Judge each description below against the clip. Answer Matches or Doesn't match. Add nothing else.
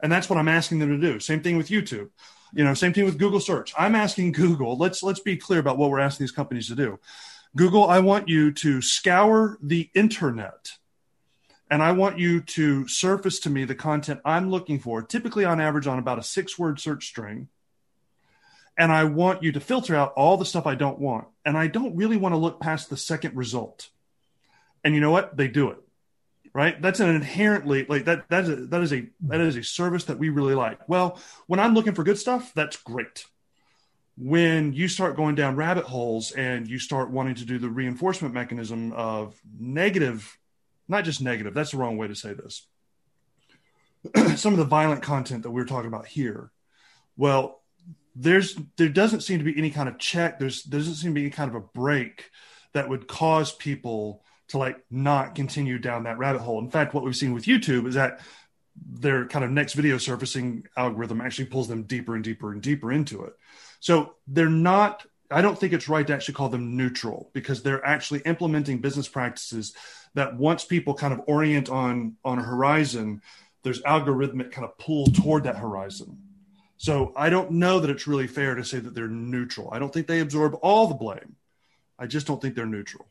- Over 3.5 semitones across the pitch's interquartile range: Matches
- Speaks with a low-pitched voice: Doesn't match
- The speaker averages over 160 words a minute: Matches